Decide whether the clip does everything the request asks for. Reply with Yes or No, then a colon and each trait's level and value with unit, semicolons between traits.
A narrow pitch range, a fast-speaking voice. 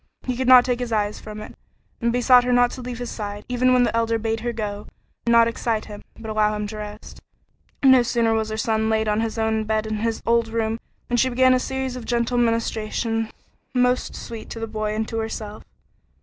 Yes: narrow, 2.0 semitones; fast, 230 wpm